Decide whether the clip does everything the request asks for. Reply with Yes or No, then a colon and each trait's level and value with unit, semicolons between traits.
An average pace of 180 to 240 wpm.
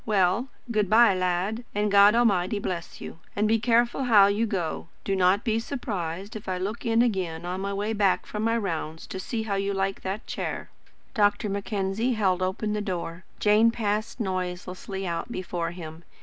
Yes: average, 185 wpm